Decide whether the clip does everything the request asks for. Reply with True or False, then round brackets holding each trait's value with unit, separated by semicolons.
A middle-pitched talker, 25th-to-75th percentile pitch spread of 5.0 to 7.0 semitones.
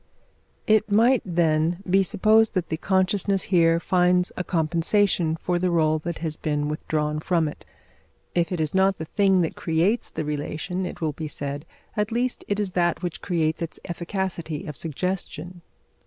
False (175 Hz; 3.2 semitones)